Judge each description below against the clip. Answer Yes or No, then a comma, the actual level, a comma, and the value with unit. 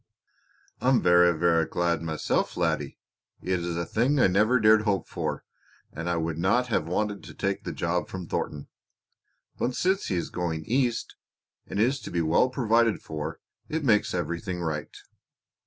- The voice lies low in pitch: Yes, very low, 95 Hz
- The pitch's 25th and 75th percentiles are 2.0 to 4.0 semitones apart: No, average, 5.3 semitones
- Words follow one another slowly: No, average, 170 wpm